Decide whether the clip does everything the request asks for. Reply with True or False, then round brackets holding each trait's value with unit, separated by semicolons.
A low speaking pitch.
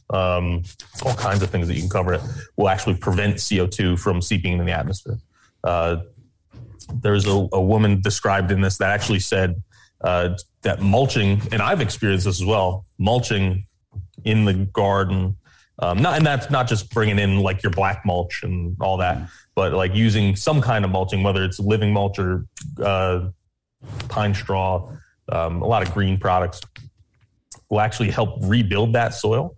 True (100 Hz)